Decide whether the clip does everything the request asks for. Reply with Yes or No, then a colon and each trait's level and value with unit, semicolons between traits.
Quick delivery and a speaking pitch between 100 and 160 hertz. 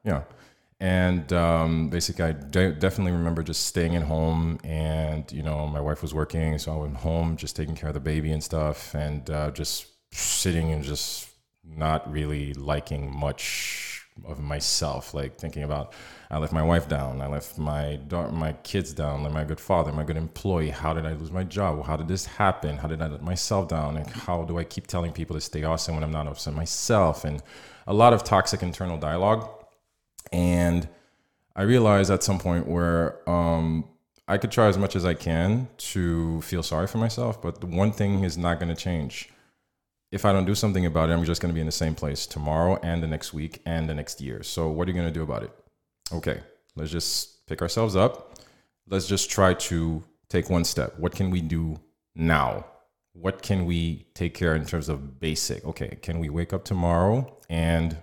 No: fast, 210 wpm; very low, 80 Hz